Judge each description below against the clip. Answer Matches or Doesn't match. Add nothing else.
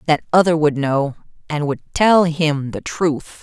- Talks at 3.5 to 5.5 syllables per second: Matches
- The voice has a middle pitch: Matches